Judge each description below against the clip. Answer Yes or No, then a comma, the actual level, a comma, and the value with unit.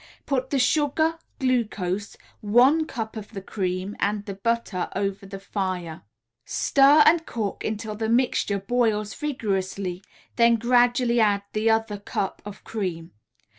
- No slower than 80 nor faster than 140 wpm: Yes, slow, 135 wpm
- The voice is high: Yes, high, 215 Hz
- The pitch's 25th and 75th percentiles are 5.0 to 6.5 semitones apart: No, average, 3.7 semitones